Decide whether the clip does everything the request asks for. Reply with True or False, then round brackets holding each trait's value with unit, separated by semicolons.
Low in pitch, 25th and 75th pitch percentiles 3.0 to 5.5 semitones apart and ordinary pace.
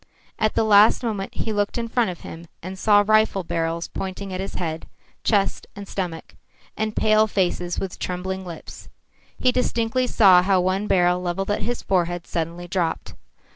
False (190 Hz; 3.3 semitones; 175 wpm)